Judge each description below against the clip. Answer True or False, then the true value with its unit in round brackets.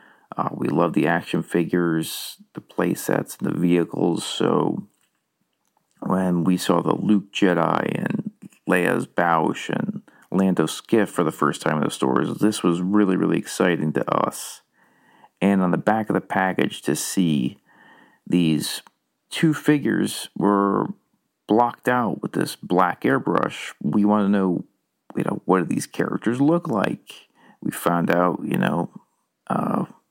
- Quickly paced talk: False (150 wpm)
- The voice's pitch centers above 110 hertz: False (95 Hz)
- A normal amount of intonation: True (3.3 semitones)